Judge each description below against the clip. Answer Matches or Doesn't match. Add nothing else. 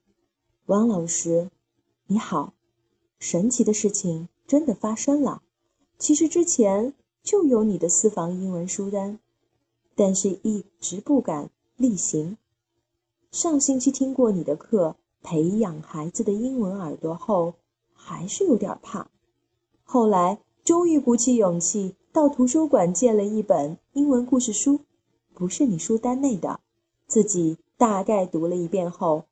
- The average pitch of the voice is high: Matches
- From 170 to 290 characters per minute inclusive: Matches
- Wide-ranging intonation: Matches